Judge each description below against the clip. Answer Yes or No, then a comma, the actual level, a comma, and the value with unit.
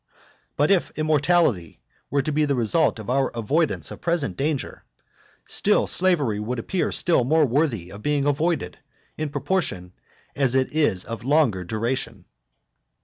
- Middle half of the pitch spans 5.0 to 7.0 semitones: Yes, average, 5.3 semitones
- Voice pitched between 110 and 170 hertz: Yes, medium, 140 Hz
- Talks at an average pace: Yes, average, 145 wpm